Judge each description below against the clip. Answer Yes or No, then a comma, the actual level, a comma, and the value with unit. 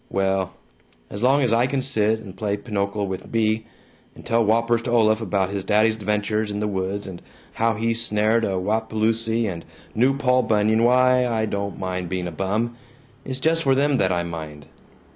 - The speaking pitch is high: No, low, 110 Hz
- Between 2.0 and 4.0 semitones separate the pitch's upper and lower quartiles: Yes, average, 2.8 semitones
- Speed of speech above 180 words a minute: Yes, average, 190 wpm